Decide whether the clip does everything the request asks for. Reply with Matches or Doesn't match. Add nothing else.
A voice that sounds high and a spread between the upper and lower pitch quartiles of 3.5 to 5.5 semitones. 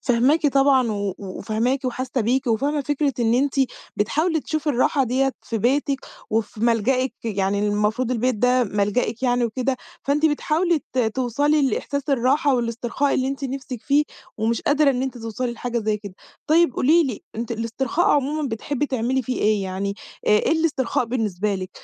Matches